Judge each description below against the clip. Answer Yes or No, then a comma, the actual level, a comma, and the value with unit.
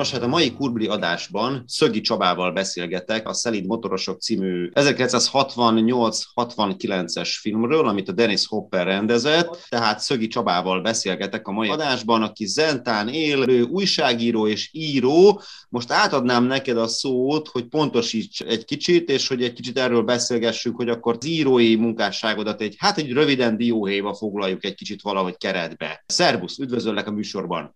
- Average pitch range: Yes, average, 3.4 semitones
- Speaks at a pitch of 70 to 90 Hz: No, low, 115 Hz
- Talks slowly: No, average, 145 wpm